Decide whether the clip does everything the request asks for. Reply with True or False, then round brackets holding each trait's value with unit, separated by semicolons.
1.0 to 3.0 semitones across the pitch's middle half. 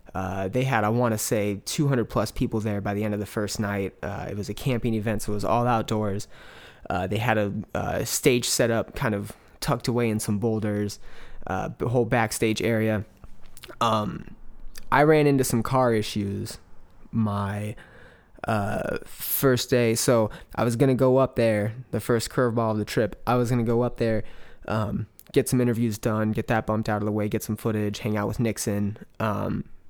True (2.5 semitones)